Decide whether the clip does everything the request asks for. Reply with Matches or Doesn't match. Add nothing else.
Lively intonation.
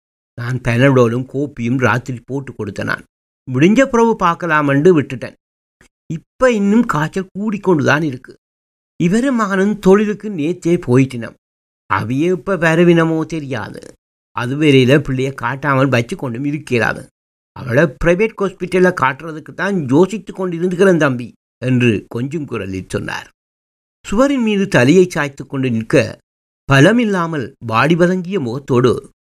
Matches